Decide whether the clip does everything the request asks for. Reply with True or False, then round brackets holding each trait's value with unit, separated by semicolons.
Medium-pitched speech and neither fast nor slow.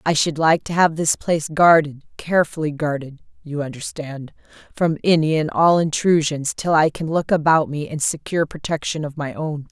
True (155 Hz; 165 wpm)